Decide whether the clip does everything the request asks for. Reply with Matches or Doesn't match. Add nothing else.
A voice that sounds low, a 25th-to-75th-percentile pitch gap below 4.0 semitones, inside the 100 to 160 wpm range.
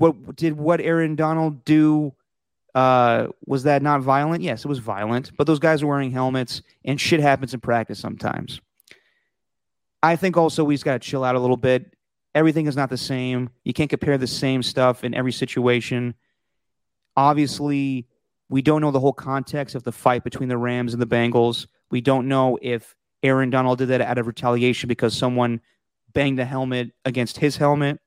Doesn't match